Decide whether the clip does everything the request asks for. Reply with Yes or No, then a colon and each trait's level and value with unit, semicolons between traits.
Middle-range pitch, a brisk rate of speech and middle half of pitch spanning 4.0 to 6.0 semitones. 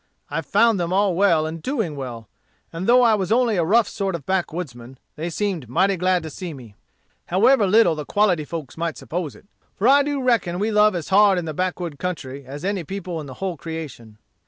Yes: medium, 180 Hz; fast, 215 wpm; average, 4.6 semitones